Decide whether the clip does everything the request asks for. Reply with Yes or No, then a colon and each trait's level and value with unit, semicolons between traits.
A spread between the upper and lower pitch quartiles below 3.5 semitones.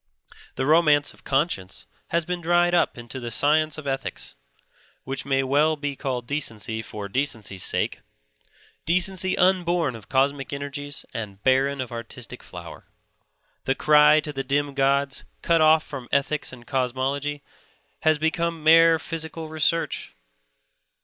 Yes: average, 3.1 semitones